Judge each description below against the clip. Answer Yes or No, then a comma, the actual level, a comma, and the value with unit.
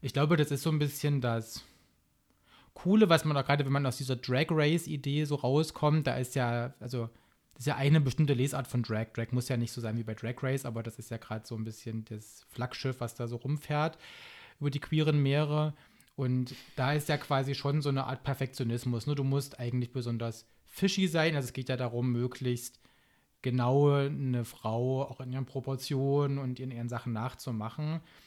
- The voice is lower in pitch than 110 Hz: No, low, 135 Hz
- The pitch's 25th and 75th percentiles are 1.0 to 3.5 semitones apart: Yes, average, 3.2 semitones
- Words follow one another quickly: Yes, fast, 205 wpm